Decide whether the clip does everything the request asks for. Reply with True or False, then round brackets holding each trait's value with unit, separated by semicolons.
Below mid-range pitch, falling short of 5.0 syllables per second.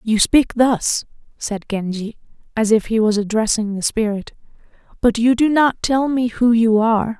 False (225 Hz; 4.5 syllables/s)